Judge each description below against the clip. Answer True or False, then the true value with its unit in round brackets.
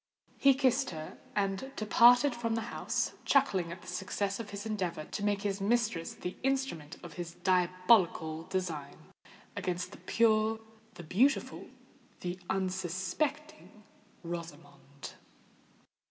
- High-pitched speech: True (195 Hz)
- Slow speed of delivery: True (115 wpm)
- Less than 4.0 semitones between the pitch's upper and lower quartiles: False (4.8 semitones)